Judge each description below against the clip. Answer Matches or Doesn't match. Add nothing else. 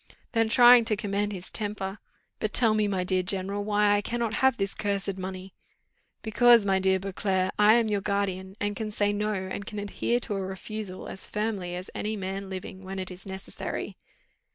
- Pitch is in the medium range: Doesn't match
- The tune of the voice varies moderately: Doesn't match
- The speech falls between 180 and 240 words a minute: Matches